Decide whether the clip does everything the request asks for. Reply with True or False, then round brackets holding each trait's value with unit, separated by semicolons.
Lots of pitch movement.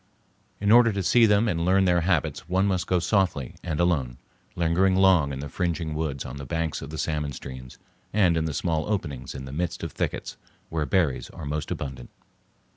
False (4.6 semitones)